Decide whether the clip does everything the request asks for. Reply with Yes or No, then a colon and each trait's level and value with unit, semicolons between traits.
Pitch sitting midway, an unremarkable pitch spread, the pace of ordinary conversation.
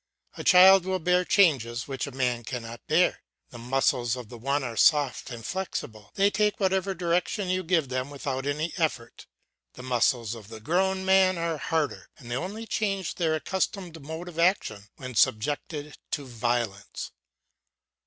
No: medium, 145 Hz; wide, 7.0 semitones; average, 165 wpm